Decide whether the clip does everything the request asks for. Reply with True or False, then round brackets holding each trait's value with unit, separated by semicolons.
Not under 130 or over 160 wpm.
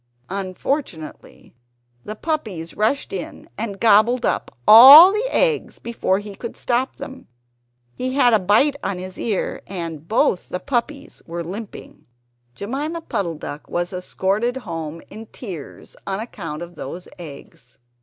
True (140 wpm)